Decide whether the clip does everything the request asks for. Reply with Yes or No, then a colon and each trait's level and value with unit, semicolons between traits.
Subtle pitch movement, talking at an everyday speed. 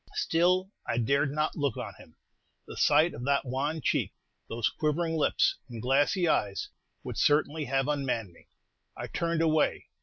No: average, 3.5 semitones; average, 160 wpm